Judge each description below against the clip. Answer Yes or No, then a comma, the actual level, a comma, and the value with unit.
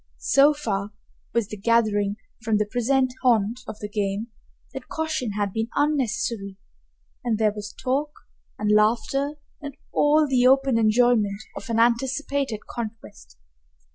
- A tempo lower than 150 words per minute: Yes, average, 140 wpm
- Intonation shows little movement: No, average, 4.0 semitones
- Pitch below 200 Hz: No, high, 230 Hz